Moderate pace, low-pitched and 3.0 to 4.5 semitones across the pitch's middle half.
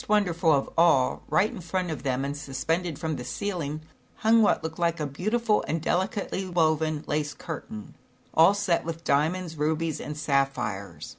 No: average, 165 wpm; medium, 160 Hz; average, 3.6 semitones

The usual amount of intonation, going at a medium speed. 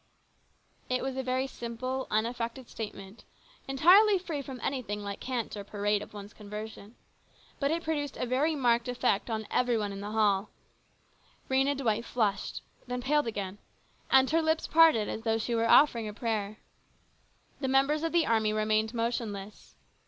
Yes: average, 3.9 semitones; average, 165 wpm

